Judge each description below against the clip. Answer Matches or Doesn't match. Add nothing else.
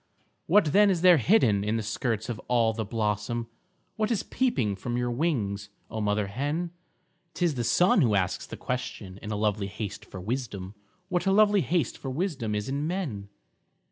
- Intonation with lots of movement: Matches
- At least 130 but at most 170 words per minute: Doesn't match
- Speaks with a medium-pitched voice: Doesn't match